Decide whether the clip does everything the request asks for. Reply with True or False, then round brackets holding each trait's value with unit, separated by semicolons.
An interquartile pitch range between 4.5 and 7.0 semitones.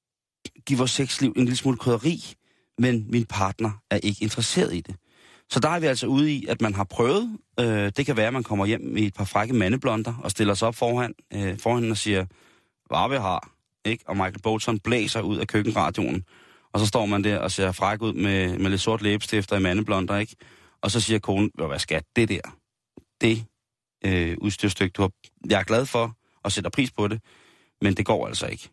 False (2.8 semitones)